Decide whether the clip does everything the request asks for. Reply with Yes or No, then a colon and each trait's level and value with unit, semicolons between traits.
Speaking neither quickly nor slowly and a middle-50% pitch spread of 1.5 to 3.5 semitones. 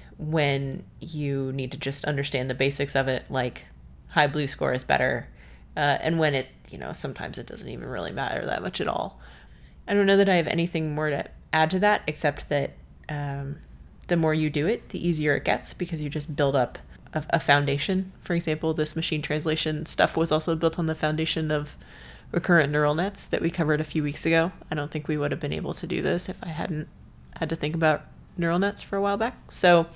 No: fast, 225 wpm; average, 2.9 semitones